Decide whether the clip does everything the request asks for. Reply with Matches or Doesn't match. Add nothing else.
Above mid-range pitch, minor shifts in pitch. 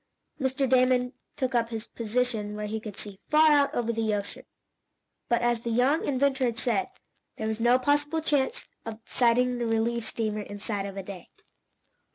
Doesn't match